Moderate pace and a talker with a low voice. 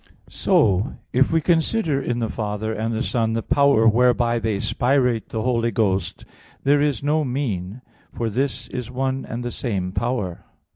Yes: average, 165 wpm; low, 120 Hz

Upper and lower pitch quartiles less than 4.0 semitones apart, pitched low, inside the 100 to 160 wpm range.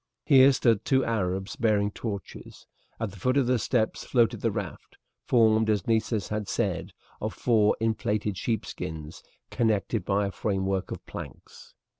Yes: narrow, 2.6 semitones; low, 110 Hz; average, 150 wpm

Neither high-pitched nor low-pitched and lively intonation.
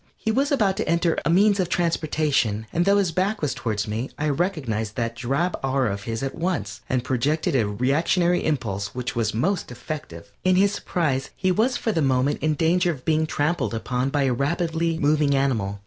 Yes: medium, 150 Hz; wide, 5.9 semitones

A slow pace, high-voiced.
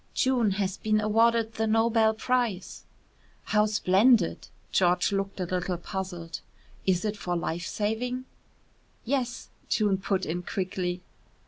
Yes: slow, 125 wpm; high, 205 Hz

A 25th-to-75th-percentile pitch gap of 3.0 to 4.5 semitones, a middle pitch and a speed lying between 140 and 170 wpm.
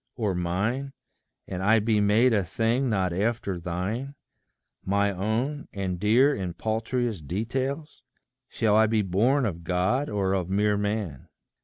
No: average, 3.9 semitones; low, 105 Hz; average, 145 wpm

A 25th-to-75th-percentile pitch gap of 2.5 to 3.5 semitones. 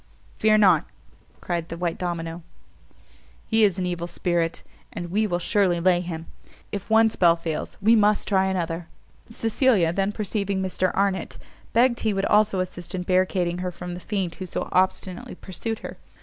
Yes: average, 2.9 semitones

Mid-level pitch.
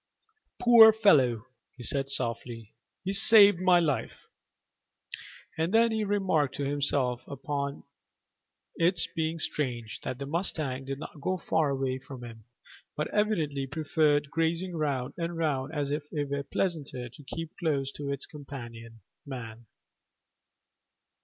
Yes: medium, 145 Hz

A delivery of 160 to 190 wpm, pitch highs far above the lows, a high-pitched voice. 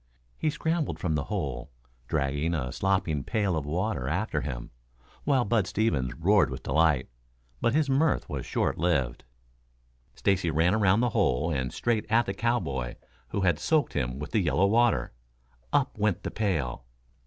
No: average, 165 wpm; wide, 7.5 semitones; very low, 90 Hz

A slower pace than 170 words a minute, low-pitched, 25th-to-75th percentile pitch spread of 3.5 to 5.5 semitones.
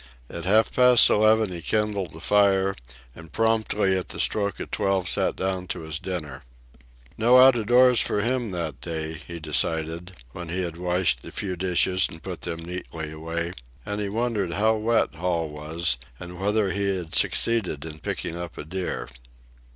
No: average, 180 wpm; very low, 90 Hz; average, 4.0 semitones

